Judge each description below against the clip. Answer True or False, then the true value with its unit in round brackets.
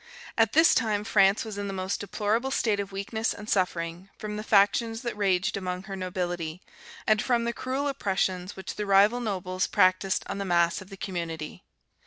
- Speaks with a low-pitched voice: False (200 Hz)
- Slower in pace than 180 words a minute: False (190 wpm)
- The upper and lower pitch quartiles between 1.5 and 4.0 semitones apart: True (2.8 semitones)